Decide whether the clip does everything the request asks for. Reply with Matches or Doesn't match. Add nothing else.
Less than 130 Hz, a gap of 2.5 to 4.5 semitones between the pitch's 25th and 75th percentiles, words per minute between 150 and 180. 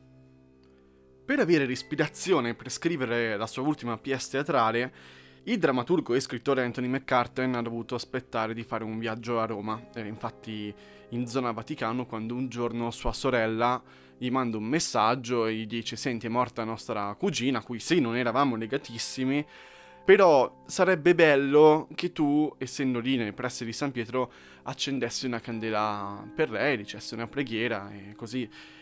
Matches